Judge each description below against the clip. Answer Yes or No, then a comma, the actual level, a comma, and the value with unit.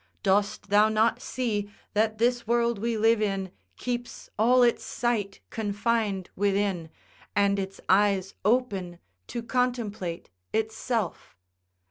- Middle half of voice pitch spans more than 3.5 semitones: No, average, 2.9 semitones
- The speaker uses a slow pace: Yes, slow, 115 wpm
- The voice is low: No, high, 215 Hz